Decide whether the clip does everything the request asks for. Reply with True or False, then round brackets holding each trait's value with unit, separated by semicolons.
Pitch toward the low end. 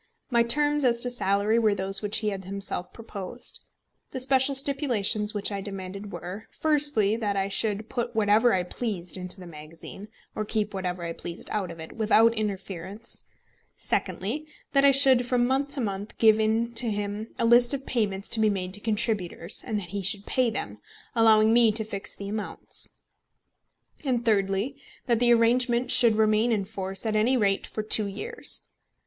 False (215 Hz)